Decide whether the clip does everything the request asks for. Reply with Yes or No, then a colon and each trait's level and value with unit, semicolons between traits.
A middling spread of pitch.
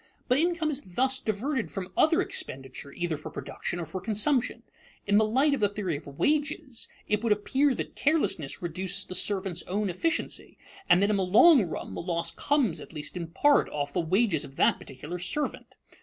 No: wide, 7.4 semitones